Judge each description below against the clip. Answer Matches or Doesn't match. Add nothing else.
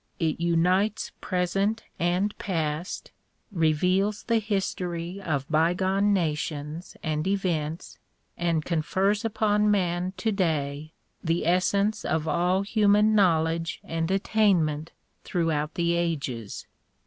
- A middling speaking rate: Doesn't match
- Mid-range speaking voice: Matches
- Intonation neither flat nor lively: Matches